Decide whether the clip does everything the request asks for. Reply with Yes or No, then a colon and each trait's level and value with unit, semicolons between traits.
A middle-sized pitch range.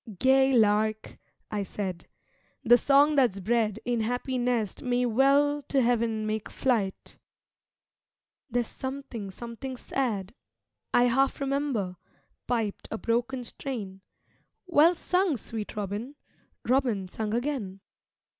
Yes: average, 4.0 semitones